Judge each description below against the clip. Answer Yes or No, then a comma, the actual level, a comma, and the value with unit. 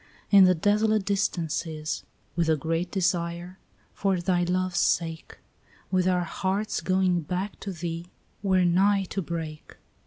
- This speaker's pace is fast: No, average, 165 wpm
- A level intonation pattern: Yes, narrow, 2.1 semitones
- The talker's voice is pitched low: No, medium, 180 Hz